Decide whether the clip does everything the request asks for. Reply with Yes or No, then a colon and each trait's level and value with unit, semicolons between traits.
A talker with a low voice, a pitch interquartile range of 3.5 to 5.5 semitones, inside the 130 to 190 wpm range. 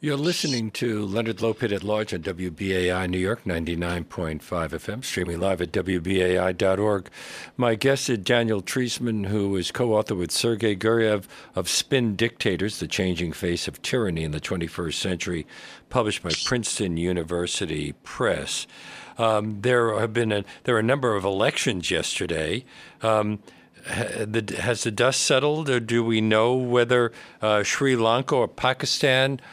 Yes: low, 105 Hz; average, 4.7 semitones; average, 145 wpm